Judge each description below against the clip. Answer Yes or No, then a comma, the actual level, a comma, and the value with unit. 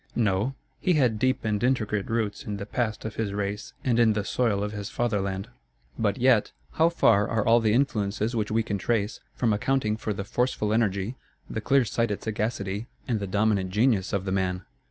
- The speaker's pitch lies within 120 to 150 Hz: No, low, 110 Hz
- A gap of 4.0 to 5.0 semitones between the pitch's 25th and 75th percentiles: No, average, 2.7 semitones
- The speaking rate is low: No, average, 195 wpm